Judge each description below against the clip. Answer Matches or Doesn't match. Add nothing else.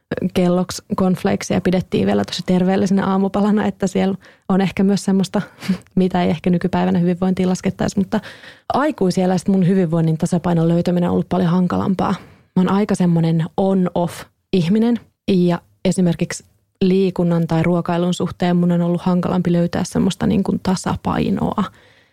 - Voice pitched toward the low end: Doesn't match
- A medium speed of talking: Matches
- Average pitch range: Doesn't match